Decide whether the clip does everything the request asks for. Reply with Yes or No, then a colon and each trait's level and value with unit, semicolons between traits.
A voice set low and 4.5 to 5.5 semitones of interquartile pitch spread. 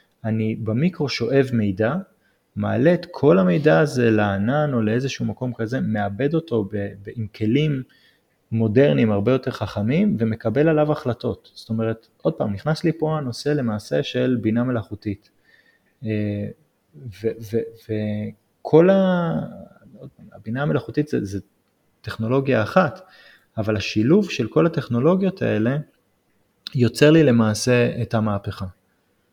Yes: low, 115 Hz; average, 5.1 semitones